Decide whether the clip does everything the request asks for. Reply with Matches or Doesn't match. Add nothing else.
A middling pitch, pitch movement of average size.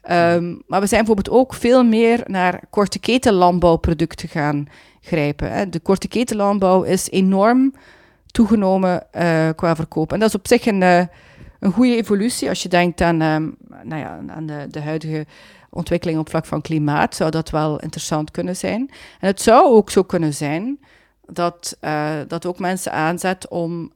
Matches